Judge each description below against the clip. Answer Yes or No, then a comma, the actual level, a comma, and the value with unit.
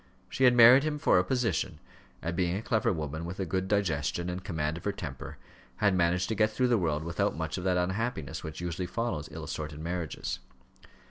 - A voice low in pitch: Yes, very low, 90 Hz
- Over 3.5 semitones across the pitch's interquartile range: Yes, average, 4.9 semitones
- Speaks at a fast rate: Yes, fast, 210 wpm